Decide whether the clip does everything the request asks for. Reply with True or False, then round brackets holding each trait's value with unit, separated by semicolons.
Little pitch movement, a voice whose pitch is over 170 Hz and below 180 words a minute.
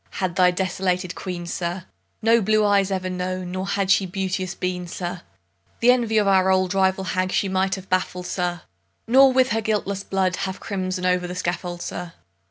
False (1.5 semitones; 185 Hz; 185 wpm)